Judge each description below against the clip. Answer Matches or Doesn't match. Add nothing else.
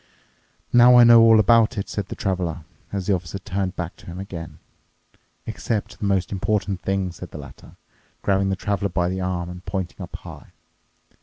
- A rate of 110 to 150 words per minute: Doesn't match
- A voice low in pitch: Matches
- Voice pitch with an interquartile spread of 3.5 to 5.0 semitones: Doesn't match